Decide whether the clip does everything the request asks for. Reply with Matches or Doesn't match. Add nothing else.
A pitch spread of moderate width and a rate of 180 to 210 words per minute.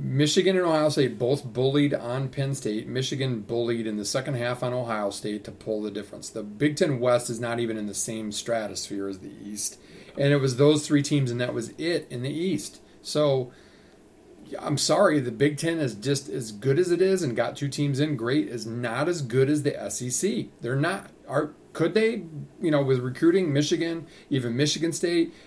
Matches